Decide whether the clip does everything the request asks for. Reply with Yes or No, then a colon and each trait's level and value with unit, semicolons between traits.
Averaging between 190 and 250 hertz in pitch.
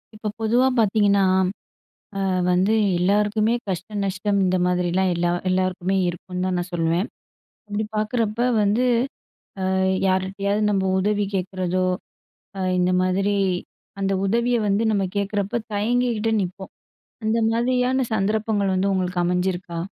Yes: high, 195 Hz